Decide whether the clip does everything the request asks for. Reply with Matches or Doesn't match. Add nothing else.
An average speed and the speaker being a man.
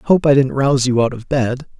Doesn't match